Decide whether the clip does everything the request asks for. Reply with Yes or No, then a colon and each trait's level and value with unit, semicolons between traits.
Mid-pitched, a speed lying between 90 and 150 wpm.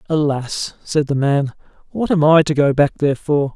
No: medium, 150 Hz; average, 200 wpm